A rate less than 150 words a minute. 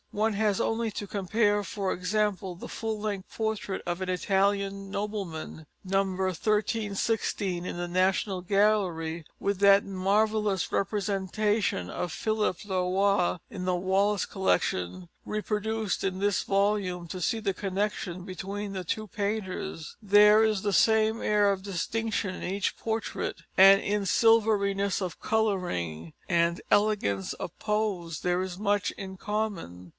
Yes: average, 140 wpm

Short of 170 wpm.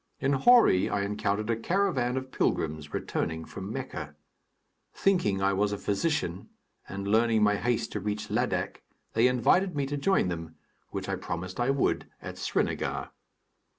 Yes: average, 155 wpm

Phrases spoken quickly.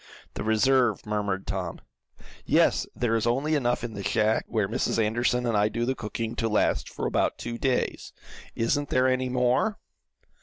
No: average, 175 wpm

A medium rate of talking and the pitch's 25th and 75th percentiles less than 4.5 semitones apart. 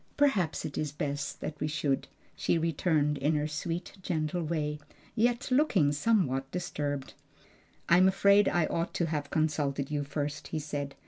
Yes: average, 150 wpm; average, 3.4 semitones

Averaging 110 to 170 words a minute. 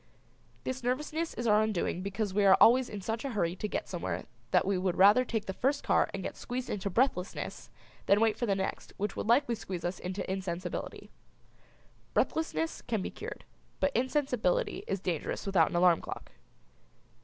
No: average, 185 wpm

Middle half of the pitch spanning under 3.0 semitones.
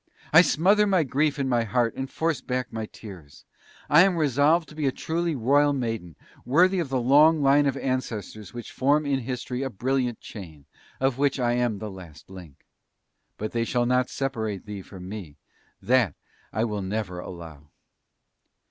No: average, 5.3 semitones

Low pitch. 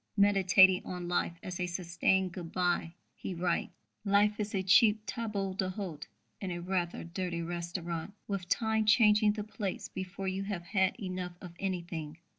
No: medium, 185 Hz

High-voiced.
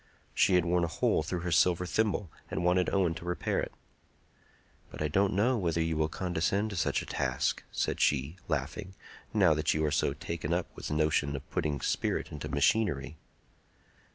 No: very low, 85 Hz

